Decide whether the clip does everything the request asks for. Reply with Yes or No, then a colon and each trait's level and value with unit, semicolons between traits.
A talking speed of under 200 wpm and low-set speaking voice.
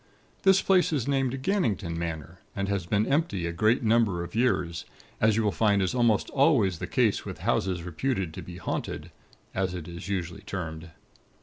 Yes: average, 185 wpm; low, 100 Hz